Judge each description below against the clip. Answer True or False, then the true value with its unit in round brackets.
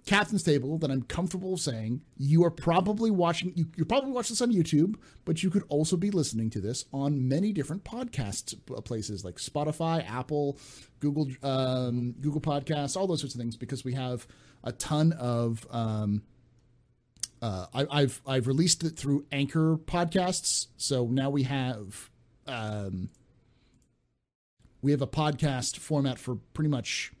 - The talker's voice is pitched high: False (140 Hz)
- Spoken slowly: False (155 wpm)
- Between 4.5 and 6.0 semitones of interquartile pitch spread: True (4.8 semitones)